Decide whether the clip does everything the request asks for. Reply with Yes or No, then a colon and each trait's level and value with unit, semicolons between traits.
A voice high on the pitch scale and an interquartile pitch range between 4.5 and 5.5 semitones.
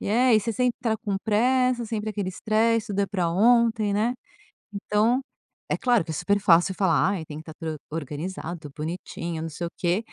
Yes: high, 205 Hz; average, 5.0 semitones